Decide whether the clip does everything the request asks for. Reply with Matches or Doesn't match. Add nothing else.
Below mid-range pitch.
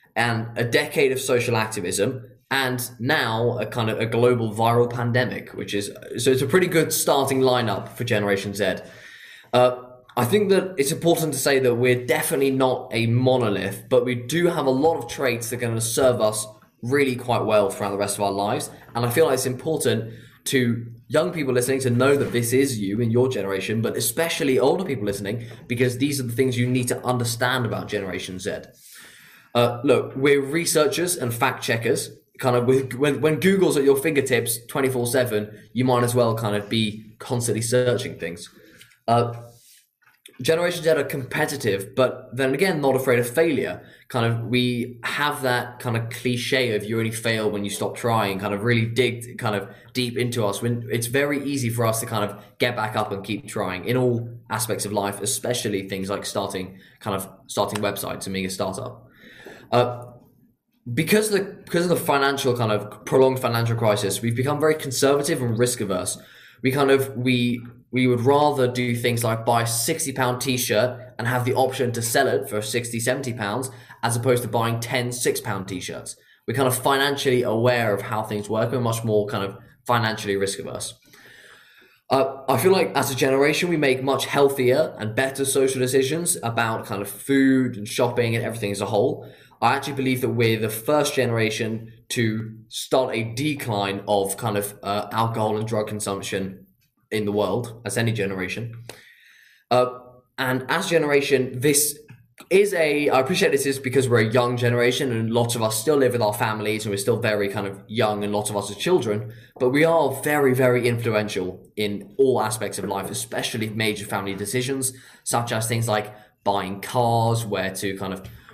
Matches